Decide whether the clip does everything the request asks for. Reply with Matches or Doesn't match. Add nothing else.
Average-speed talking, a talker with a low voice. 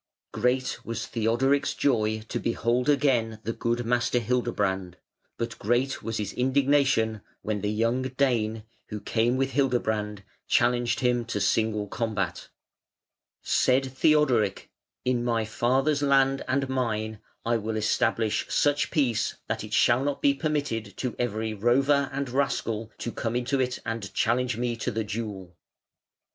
Matches